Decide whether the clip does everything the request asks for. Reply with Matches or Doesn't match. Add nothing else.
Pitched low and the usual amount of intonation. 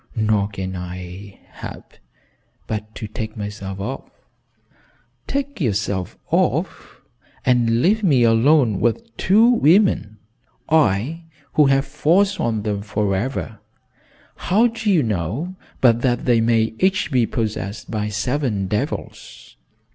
Doesn't match